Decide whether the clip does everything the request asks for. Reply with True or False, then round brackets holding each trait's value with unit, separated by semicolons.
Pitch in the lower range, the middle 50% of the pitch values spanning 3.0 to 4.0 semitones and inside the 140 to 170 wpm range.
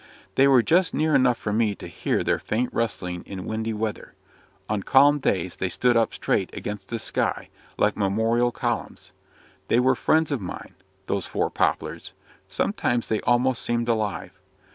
True (115 Hz; 3.3 semitones; 165 wpm)